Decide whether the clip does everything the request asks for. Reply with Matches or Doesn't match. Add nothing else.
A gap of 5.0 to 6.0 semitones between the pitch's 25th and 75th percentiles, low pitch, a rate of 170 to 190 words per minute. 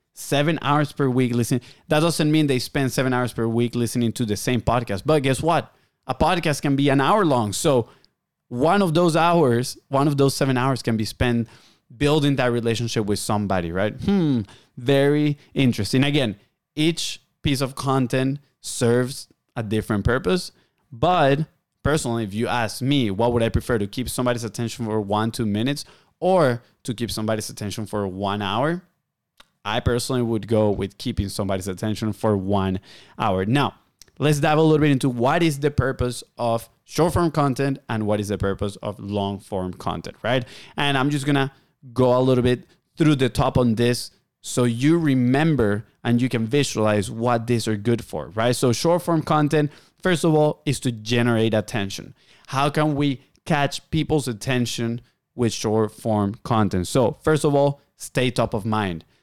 Doesn't match